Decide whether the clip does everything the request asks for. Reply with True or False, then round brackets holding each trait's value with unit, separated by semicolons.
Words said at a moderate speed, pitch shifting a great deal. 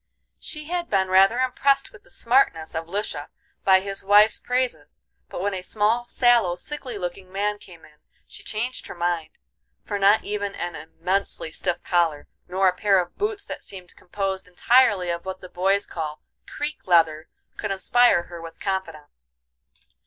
False (165 wpm; 3.8 semitones)